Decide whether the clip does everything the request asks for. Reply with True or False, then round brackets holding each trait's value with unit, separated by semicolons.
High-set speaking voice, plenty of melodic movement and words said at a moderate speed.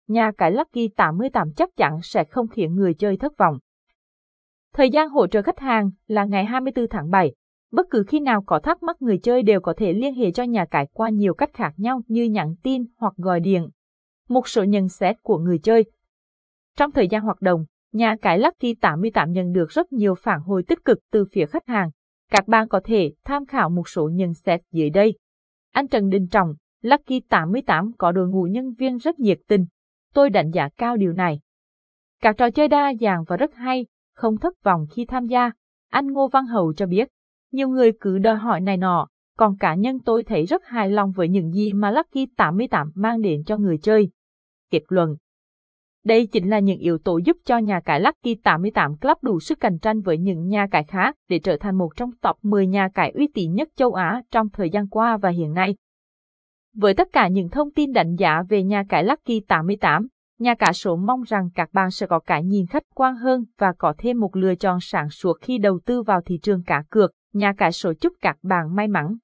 False (210 Hz; 4.8 semitones; 220 wpm)